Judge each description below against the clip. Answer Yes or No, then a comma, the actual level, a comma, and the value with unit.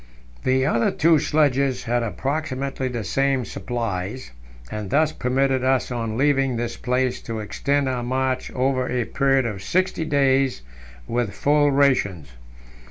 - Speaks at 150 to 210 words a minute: No, average, 140 wpm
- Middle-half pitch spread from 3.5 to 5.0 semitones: No, narrow, 2.6 semitones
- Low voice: Yes, low, 130 Hz